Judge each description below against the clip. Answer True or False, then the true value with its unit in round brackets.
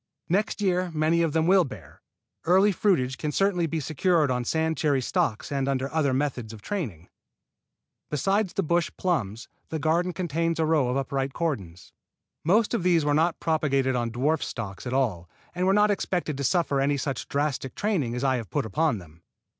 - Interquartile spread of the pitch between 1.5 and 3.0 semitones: False (4.9 semitones)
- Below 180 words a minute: False (190 wpm)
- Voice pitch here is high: False (150 Hz)